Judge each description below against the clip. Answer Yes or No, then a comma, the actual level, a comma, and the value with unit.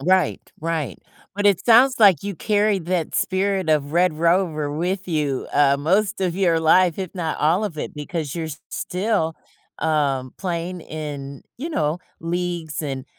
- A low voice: No, medium, 170 Hz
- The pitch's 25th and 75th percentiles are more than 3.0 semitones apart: Yes, average, 3.8 semitones